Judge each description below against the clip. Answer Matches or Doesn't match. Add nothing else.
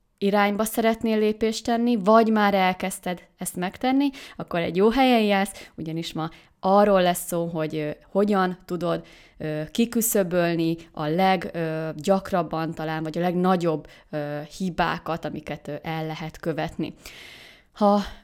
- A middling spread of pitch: Matches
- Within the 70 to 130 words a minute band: Matches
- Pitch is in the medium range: Matches